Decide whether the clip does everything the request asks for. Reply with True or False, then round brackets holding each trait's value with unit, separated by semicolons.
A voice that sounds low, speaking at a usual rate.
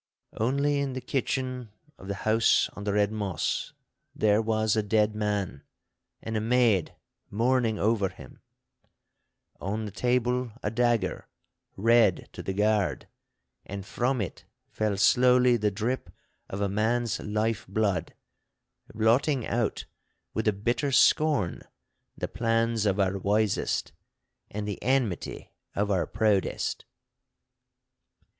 False (110 Hz; 125 wpm)